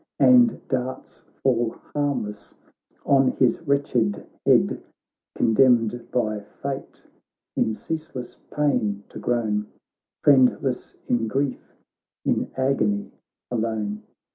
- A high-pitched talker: No, low, 125 Hz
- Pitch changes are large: No, average, 4.0 semitones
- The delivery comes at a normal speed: No, slow, 90 wpm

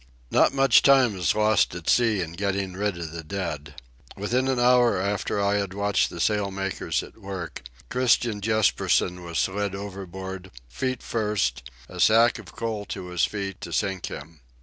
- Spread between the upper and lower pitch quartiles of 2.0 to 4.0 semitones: Yes, average, 3.3 semitones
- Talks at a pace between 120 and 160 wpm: No, average, 170 wpm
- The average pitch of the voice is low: Yes, low, 100 Hz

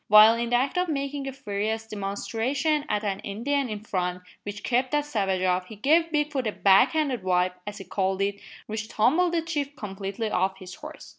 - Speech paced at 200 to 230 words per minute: Yes, fast, 205 wpm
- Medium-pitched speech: No, high, 220 Hz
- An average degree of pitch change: No, wide, 6.2 semitones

